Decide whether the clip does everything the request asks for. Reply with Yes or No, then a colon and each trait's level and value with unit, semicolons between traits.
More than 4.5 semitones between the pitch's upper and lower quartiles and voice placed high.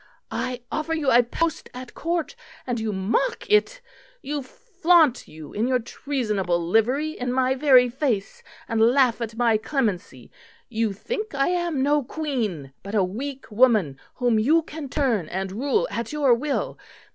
Yes: wide, 5.4 semitones; very high, 250 Hz